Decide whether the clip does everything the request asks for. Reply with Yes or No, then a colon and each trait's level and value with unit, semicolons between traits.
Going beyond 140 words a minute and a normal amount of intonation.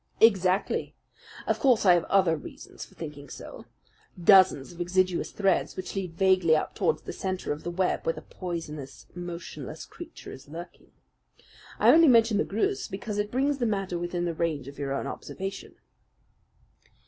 Yes: average, 170 wpm; average, 3.3 semitones